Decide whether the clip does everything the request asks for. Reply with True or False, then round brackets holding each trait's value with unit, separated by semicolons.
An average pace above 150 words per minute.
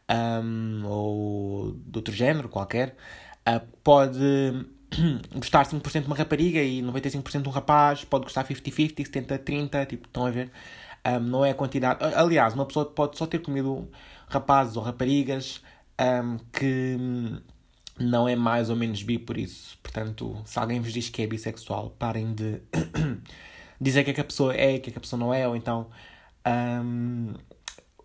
True (170 wpm)